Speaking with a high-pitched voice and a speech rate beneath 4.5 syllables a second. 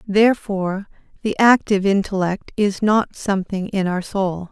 No: high, 200 Hz; 4.8 syllables/s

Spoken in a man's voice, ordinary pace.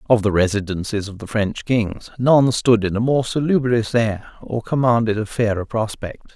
Yes: male; average, 180 wpm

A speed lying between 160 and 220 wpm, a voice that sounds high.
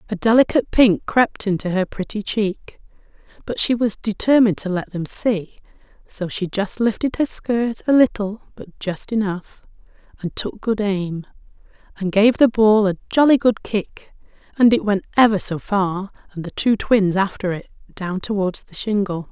Yes: average, 170 wpm; high, 205 Hz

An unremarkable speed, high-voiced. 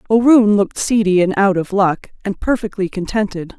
Yes: average, 165 wpm; high, 200 Hz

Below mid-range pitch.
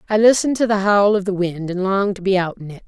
No: high, 195 Hz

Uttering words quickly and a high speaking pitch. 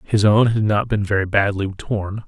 No: fast, 210 wpm; low, 105 Hz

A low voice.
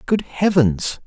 No: medium, 160 Hz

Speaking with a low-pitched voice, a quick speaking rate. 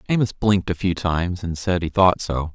Yes: very low, 90 Hz; fast, 235 wpm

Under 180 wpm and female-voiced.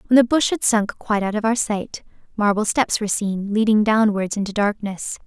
No: fast, 205 wpm; female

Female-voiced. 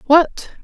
Yes: female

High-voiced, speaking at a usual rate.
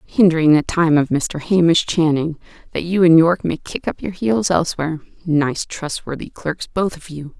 No: medium, 165 Hz; average, 185 wpm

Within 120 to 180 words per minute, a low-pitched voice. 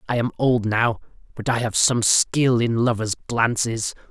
Yes: average, 175 wpm; low, 115 Hz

